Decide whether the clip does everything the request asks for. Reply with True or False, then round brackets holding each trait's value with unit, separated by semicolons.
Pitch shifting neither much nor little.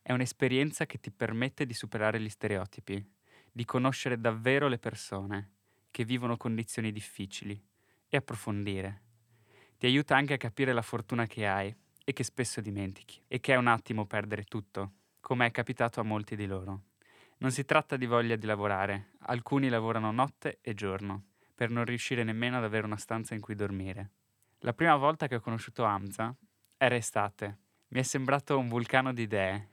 True (3.7 semitones)